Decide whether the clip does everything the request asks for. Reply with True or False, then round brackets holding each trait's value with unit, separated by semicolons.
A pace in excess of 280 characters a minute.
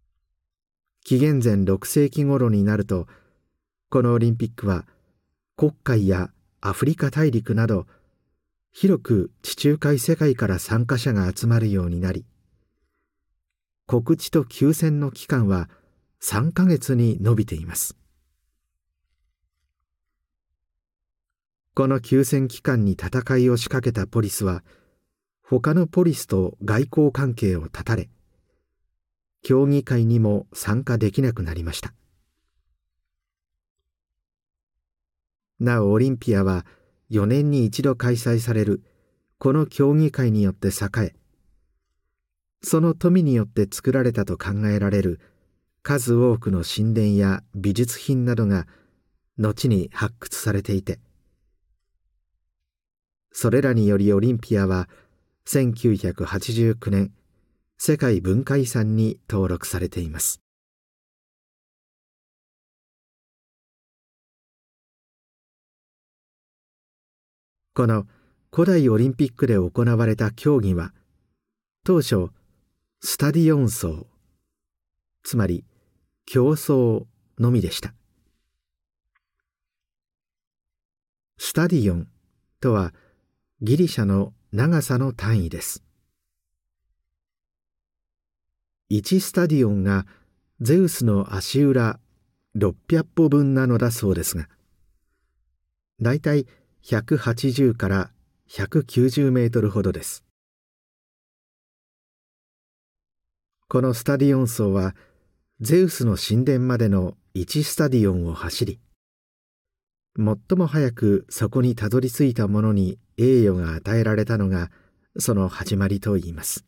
False (190 characters per minute)